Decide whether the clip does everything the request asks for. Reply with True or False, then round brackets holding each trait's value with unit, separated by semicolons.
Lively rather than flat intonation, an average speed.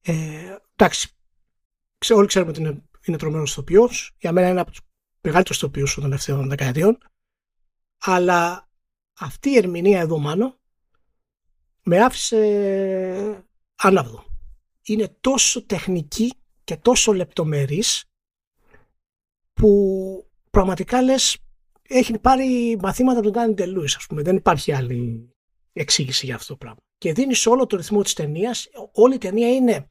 True (6.4 semitones; 130 wpm)